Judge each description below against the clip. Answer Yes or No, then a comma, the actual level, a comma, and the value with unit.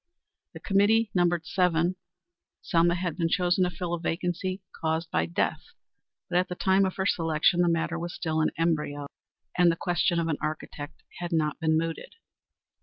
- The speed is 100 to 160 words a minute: No, average, 180 wpm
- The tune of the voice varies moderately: No, narrow, 1.7 semitones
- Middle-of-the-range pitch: Yes, medium, 170 Hz